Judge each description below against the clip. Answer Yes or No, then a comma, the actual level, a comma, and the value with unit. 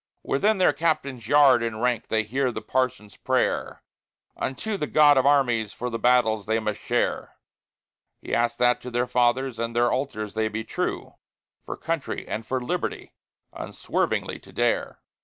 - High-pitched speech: No, low, 125 Hz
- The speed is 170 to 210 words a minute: No, average, 160 wpm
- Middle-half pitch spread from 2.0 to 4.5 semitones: Yes, average, 3.3 semitones